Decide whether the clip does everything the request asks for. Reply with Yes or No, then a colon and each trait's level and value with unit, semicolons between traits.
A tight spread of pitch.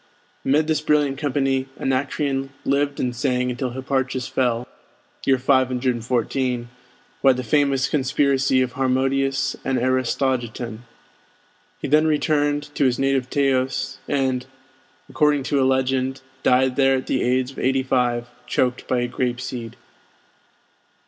Yes: narrow, 1.4 semitones